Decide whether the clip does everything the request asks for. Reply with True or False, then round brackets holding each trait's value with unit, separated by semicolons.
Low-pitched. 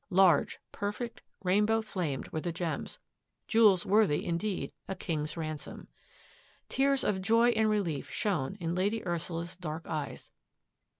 False (185 Hz)